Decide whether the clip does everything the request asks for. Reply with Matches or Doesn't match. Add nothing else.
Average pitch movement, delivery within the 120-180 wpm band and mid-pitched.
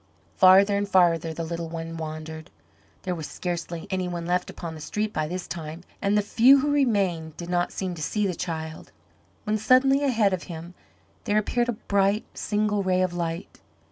Doesn't match